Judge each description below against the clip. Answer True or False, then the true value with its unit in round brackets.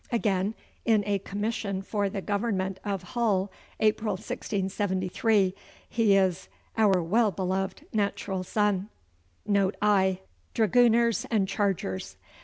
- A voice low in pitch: False (200 Hz)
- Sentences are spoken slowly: True (110 wpm)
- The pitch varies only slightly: True (2.3 semitones)